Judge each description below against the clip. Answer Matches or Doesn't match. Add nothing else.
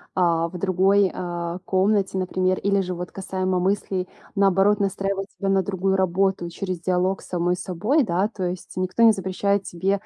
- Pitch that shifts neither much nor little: Doesn't match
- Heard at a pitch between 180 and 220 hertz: Matches